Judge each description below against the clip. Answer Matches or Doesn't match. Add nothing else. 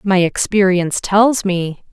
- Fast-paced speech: Doesn't match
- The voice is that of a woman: Matches